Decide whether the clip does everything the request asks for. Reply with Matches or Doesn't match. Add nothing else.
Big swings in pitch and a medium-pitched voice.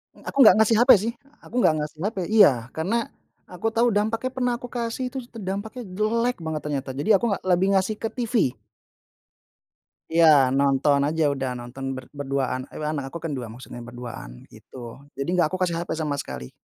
Matches